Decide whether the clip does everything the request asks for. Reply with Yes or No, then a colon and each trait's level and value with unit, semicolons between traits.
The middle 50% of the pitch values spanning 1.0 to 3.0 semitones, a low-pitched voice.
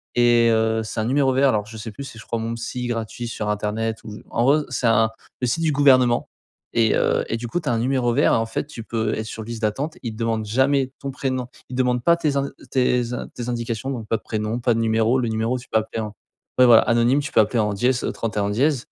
Yes: narrow, 2.6 semitones; low, 120 Hz